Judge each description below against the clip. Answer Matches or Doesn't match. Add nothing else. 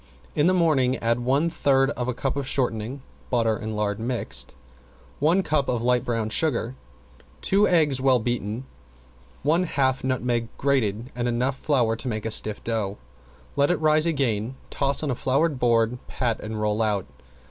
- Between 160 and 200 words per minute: Matches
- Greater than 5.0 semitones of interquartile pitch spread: Doesn't match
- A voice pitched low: Matches